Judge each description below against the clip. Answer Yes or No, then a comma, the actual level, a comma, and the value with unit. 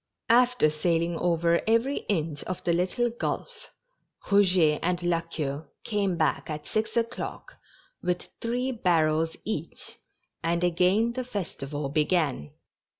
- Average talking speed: No, slow, 130 wpm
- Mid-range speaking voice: Yes, medium, 175 Hz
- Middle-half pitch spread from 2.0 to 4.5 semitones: No, wide, 5.5 semitones